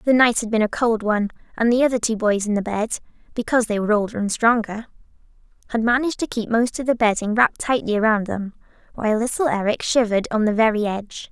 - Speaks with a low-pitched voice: No, high, 225 Hz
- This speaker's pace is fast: Yes, fast, 220 wpm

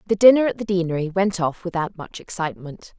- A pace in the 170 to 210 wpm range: Yes, average, 200 wpm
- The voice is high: No, medium, 180 Hz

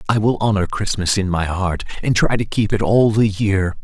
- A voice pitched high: No, low, 100 Hz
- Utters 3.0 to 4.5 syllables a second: No, 5.0 syllables/s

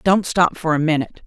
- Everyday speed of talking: No, fast, 235 wpm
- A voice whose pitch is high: No, medium, 165 Hz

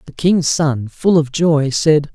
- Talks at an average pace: Yes, average, 195 wpm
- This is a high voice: No, medium, 150 Hz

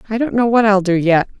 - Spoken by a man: No, female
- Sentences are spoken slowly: No, fast, 300 wpm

